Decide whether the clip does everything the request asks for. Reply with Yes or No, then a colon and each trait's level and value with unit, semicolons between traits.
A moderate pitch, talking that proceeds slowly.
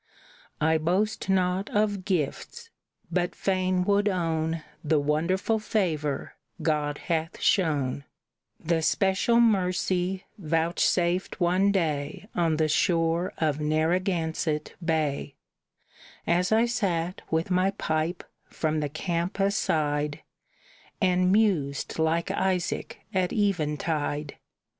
Yes: medium, 170 Hz; slow, 105 wpm